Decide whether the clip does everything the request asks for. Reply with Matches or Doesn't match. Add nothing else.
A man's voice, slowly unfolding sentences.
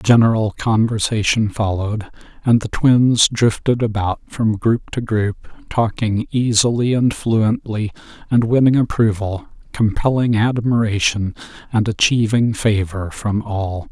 Matches